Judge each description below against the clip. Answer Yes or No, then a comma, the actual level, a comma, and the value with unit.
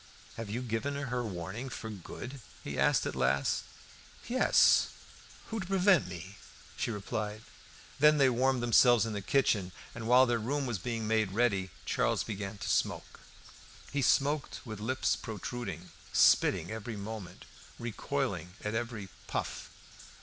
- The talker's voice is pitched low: Yes, low, 115 Hz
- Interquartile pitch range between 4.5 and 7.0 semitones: No, average, 4.1 semitones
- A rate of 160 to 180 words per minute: No, average, 145 wpm